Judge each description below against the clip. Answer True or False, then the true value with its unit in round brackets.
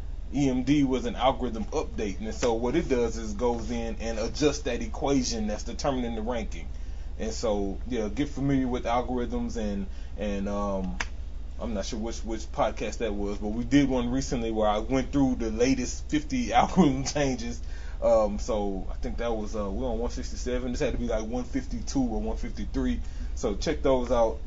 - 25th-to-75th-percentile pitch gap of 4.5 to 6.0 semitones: True (4.8 semitones)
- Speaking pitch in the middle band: False (120 Hz)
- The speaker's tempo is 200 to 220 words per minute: False (185 wpm)